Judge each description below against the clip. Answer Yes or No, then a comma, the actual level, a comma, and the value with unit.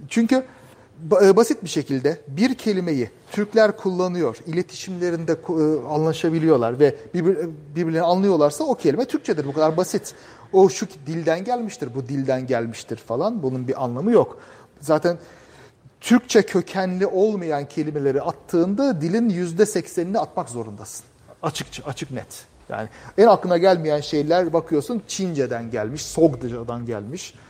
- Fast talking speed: No, average, 120 wpm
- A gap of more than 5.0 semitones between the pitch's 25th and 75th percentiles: Yes, wide, 5.4 semitones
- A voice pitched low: No, medium, 165 Hz